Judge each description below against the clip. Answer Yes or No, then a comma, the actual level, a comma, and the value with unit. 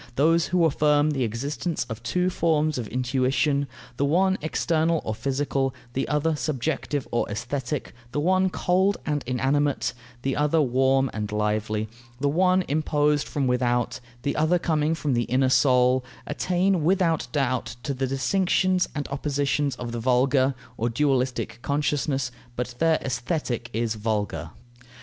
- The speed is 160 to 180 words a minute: No, average, 145 wpm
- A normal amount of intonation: Yes, average, 3.9 semitones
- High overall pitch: No, medium, 140 Hz